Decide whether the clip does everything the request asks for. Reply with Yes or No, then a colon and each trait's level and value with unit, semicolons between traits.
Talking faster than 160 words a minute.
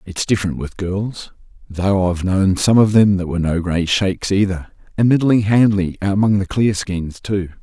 Yes: average, 175 wpm